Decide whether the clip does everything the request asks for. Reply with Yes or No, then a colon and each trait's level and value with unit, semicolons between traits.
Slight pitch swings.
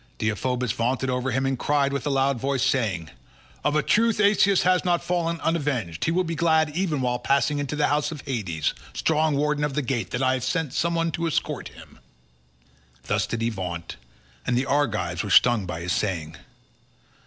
No: average, 5.2 semitones